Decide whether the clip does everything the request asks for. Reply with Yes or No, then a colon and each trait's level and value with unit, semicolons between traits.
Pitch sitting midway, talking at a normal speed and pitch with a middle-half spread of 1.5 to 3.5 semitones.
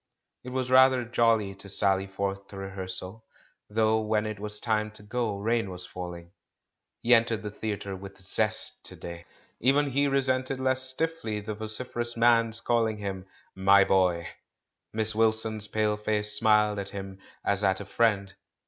No: low, 105 Hz; average, 160 wpm; average, 2.9 semitones